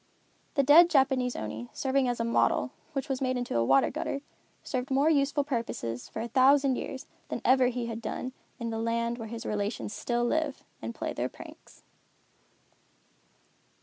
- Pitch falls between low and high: No, very high, 250 Hz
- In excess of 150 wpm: Yes, average, 175 wpm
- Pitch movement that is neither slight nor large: Yes, average, 3.0 semitones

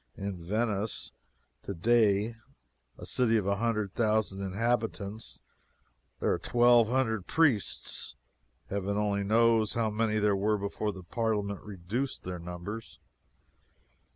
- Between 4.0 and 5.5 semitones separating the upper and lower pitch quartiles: No, narrow, 2.4 semitones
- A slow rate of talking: Yes, slow, 120 wpm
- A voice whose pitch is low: Yes, low, 105 Hz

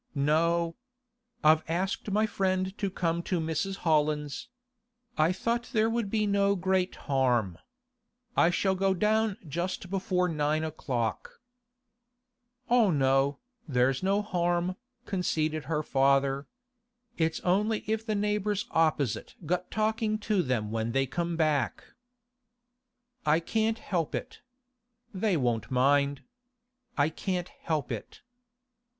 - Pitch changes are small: No, average, 5.2 semitones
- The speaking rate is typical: No, slow, 120 wpm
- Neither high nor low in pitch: Yes, medium, 170 Hz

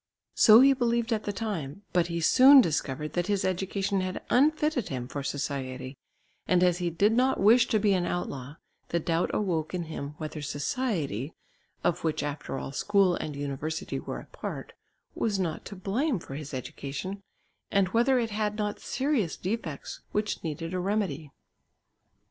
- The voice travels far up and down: Yes, wide, 5.9 semitones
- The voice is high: No, medium, 180 Hz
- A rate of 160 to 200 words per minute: Yes, average, 170 wpm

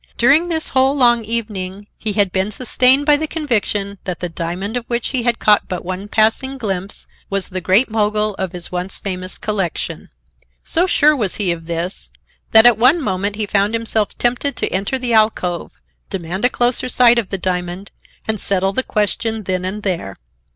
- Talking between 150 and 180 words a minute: No, average, 190 wpm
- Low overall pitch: No, high, 210 Hz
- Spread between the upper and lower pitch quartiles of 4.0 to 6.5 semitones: Yes, average, 4.4 semitones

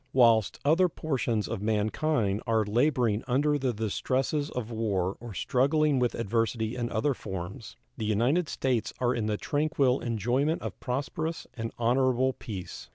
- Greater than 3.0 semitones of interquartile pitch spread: Yes, average, 3.6 semitones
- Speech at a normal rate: Yes, average, 150 wpm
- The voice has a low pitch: Yes, low, 120 Hz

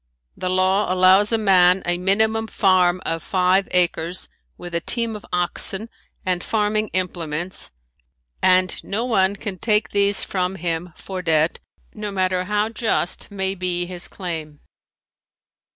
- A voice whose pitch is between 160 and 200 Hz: Yes, medium, 185 Hz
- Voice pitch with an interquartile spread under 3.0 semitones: Yes, narrow, 2.4 semitones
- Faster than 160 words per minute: No, average, 140 wpm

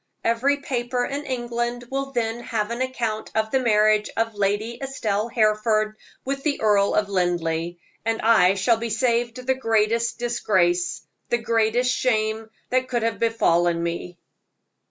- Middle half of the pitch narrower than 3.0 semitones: Yes, narrow, 2.4 semitones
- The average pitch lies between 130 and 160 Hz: No, high, 225 Hz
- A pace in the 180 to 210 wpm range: No, average, 150 wpm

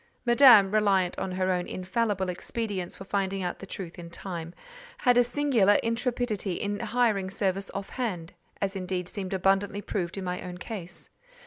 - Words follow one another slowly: No, average, 155 wpm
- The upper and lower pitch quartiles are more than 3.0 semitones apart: Yes, average, 3.5 semitones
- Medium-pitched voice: No, high, 195 Hz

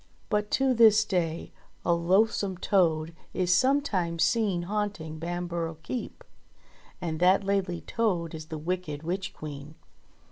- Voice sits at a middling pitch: Yes, medium, 180 Hz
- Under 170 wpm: Yes, slow, 135 wpm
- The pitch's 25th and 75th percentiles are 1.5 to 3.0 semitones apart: No, average, 3.7 semitones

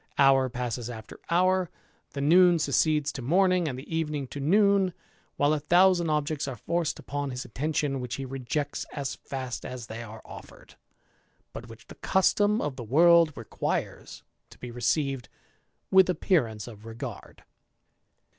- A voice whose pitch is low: No, medium, 145 Hz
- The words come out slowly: No, average, 155 wpm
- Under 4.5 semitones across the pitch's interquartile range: No, average, 5.2 semitones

